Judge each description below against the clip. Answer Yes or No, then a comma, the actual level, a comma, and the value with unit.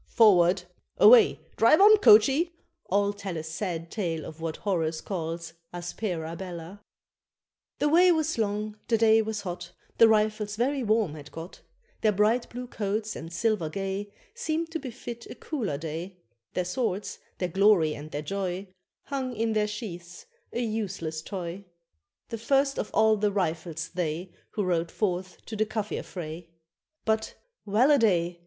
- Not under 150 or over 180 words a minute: Yes, average, 160 wpm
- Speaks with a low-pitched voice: No, high, 200 Hz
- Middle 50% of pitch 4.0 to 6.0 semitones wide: Yes, average, 4.6 semitones